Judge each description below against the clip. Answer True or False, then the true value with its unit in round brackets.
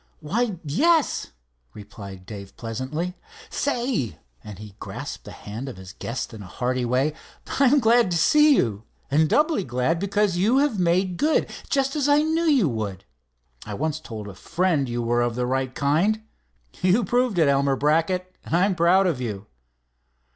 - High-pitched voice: False (160 Hz)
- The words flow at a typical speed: True (175 wpm)